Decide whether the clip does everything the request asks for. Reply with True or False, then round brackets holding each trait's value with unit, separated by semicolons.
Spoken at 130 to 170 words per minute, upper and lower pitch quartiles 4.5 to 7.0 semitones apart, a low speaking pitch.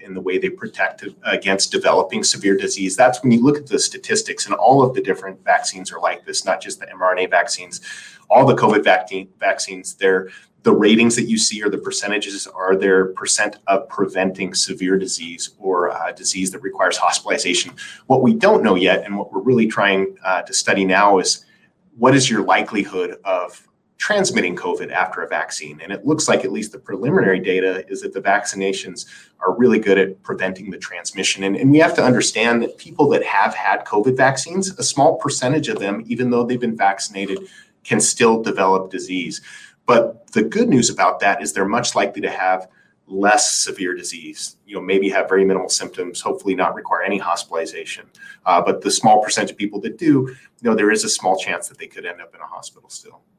False (205 wpm; 5.6 semitones; 100 Hz)